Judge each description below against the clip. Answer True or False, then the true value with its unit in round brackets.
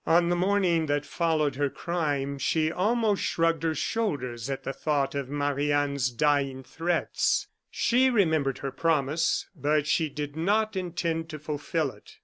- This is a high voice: False (155 Hz)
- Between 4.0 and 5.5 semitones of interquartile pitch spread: False (3.3 semitones)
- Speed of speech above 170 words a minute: False (155 wpm)